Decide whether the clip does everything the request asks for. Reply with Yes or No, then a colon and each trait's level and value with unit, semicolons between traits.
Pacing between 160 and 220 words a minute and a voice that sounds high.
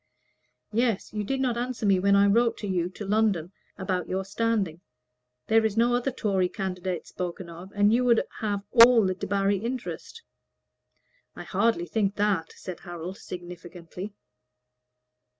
No: average, 150 wpm; high, 200 Hz